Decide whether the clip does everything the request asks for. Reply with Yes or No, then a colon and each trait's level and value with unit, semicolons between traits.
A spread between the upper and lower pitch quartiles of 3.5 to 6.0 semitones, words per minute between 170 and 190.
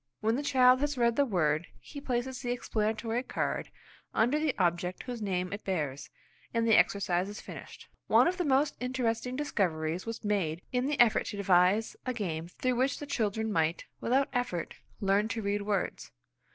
Yes: average, 5.2 semitones; average, 180 wpm